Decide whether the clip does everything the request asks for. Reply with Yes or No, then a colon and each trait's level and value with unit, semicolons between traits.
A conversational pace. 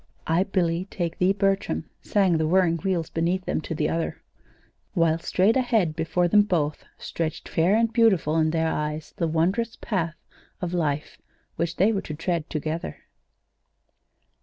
Yes: average, 160 wpm